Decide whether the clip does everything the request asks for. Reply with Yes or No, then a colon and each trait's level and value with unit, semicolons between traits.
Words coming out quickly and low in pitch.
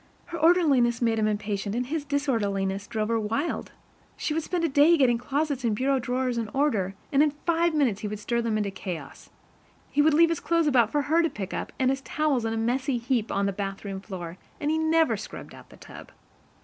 No: fast, 225 wpm; high, 245 Hz